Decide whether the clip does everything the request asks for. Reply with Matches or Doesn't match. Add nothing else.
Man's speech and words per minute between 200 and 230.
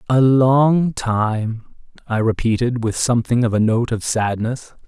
Doesn't match